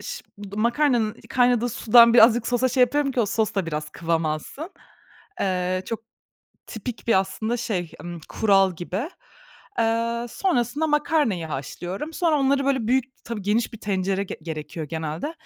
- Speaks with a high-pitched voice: Yes, high, 225 Hz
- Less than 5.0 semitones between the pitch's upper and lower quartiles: No, average, 5.3 semitones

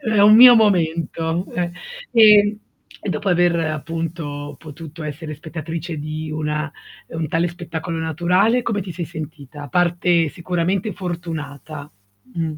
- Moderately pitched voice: Yes, medium, 165 Hz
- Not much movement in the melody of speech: Yes, narrow, 2.3 semitones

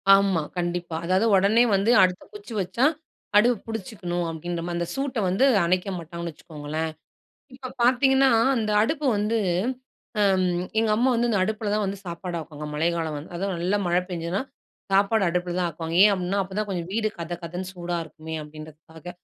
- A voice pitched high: No, medium, 180 Hz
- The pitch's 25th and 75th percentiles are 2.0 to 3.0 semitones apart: No, average, 3.9 semitones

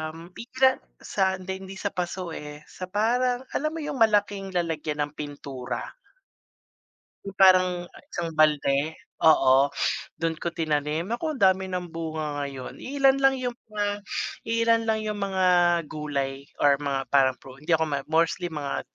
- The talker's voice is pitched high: No, medium, 175 Hz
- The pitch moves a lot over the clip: Yes, wide, 5.9 semitones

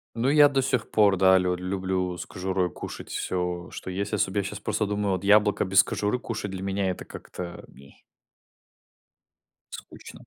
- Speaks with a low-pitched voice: Yes, very low, 95 Hz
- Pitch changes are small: Yes, narrow, 2.2 semitones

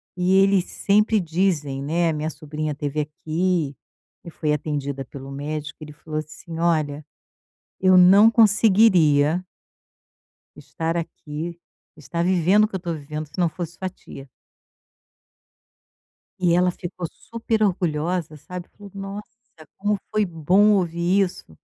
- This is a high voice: No, medium, 170 Hz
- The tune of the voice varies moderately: Yes, average, 3.7 semitones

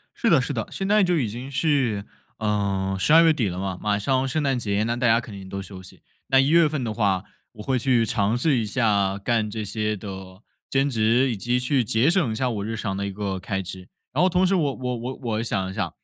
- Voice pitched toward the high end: No, low, 115 Hz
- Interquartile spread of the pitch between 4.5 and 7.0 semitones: Yes, average, 4.8 semitones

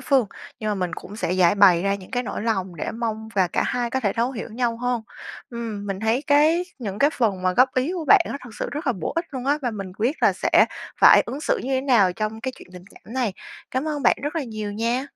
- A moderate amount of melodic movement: Yes, average, 4.5 semitones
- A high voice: Yes, high, 230 Hz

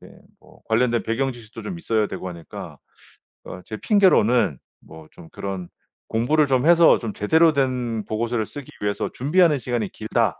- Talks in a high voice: No, low, 120 Hz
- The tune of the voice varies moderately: Yes, average, 4.7 semitones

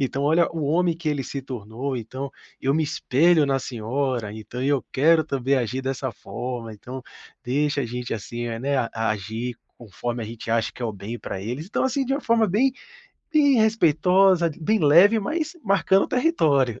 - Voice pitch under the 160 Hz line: Yes, low, 135 Hz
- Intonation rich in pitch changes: Yes, wide, 6.3 semitones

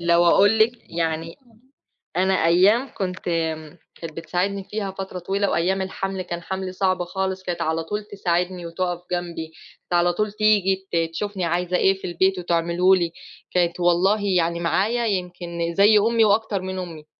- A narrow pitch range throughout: Yes, narrow, 2.2 semitones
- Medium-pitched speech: Yes, medium, 180 Hz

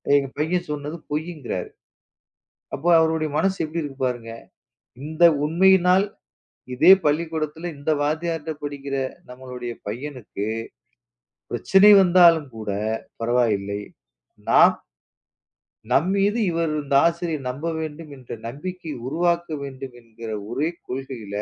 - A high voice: No, medium, 150 Hz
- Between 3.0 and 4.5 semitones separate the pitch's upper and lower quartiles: No, average, 4.9 semitones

